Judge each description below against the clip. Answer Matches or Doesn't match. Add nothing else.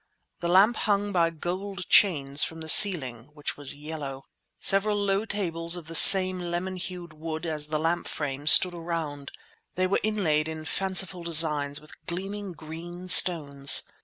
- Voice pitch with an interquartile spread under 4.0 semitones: Matches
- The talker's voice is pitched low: Doesn't match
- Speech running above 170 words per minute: Doesn't match